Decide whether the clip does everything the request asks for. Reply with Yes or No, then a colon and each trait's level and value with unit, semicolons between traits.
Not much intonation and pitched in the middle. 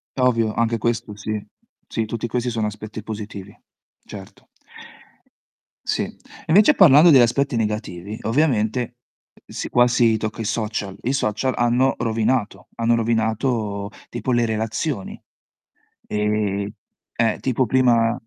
No: narrow, 2.3 semitones; low, 115 Hz